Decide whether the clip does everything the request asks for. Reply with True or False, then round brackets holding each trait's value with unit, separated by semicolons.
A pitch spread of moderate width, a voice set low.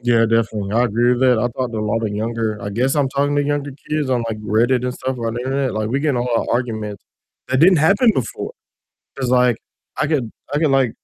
True (3.1 semitones; 125 Hz)